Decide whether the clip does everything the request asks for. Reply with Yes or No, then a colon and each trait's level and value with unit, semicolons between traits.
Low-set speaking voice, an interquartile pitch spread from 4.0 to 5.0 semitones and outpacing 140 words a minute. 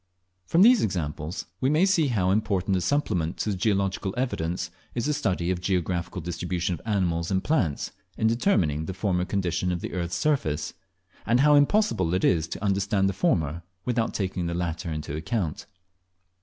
Yes: very low, 95 Hz; average, 4.6 semitones; average, 175 wpm